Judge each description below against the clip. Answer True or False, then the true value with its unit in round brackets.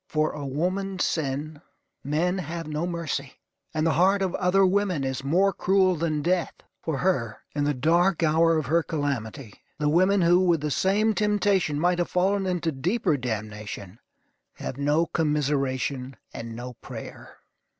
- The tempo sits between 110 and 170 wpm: True (160 wpm)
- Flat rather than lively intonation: False (4.4 semitones)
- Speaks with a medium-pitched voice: True (160 Hz)